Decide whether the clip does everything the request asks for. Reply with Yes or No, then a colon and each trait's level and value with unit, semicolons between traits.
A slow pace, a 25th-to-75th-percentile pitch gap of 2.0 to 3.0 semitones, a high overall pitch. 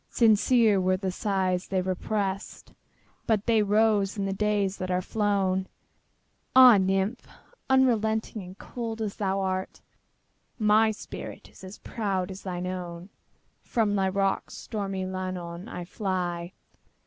Yes: slow, 115 wpm; narrow, 2.4 semitones; high, 195 Hz